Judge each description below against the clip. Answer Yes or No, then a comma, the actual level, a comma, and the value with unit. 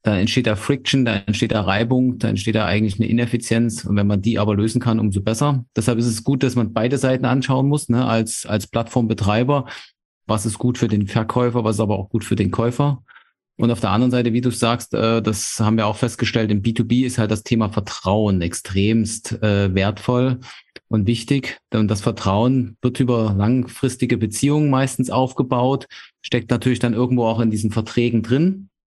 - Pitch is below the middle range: Yes, low, 115 Hz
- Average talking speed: Yes, average, 195 wpm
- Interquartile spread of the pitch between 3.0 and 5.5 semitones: No, narrow, 2.4 semitones